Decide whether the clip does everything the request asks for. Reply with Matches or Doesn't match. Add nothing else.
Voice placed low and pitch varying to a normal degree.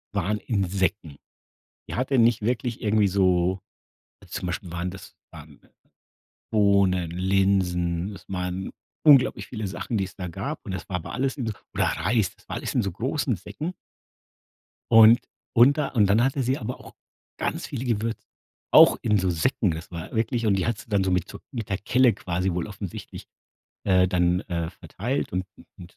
Matches